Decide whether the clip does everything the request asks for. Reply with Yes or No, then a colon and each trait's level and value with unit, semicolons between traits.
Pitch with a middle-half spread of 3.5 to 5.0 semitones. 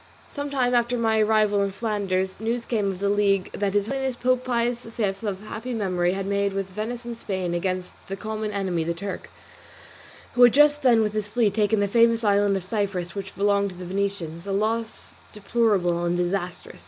No: average, 3.0 semitones